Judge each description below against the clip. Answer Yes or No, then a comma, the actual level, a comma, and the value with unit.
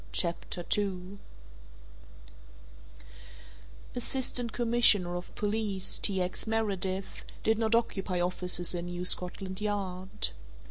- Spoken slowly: Yes, slow, 95 wpm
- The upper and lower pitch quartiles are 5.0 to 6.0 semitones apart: No, average, 3.4 semitones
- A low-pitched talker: No, high, 195 Hz